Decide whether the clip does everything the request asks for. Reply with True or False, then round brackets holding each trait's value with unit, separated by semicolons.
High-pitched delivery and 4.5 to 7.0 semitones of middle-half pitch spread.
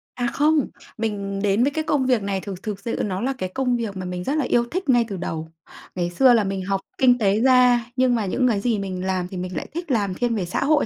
True (220 Hz; 4.9 semitones)